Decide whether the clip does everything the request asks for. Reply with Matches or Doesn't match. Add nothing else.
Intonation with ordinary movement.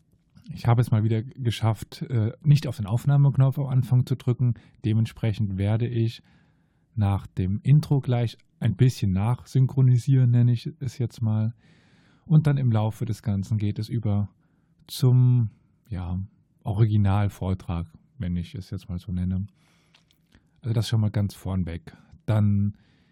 Matches